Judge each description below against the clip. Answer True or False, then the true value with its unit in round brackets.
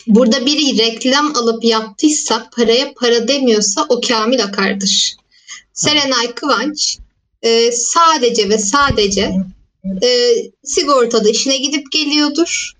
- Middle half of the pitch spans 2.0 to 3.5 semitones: False (4.7 semitones)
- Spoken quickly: False (100 wpm)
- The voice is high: True (245 Hz)